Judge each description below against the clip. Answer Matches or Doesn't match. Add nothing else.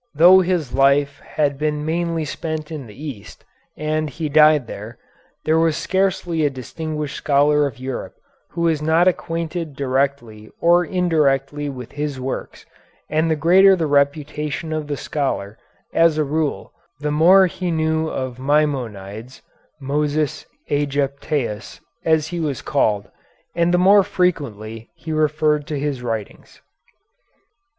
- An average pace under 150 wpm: Matches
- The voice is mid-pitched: Matches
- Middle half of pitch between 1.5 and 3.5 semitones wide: Matches